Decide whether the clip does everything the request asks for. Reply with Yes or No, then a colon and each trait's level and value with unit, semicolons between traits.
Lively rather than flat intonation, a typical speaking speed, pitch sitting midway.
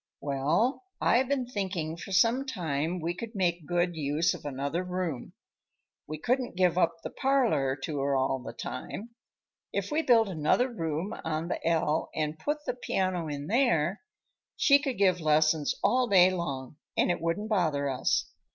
Yes: wide, 6.2 semitones; average, 170 wpm; medium, 175 Hz